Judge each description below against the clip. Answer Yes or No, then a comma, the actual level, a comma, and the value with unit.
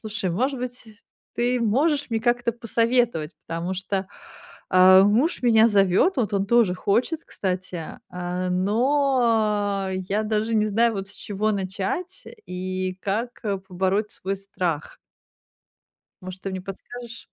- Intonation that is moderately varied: Yes, average, 4.0 semitones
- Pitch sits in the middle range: No, high, 205 Hz